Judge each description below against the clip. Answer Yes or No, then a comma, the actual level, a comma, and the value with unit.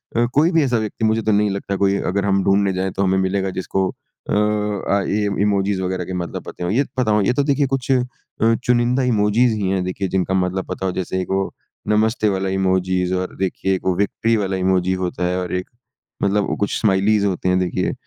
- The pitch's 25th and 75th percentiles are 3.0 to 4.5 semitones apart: No, narrow, 2.5 semitones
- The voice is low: Yes, low, 100 Hz